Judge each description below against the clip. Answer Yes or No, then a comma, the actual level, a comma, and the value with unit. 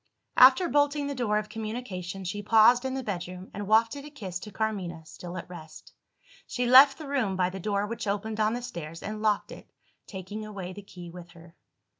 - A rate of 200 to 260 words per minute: Yes, fast, 205 wpm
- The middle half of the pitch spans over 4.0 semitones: Yes, average, 4.8 semitones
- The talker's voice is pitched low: No, high, 210 Hz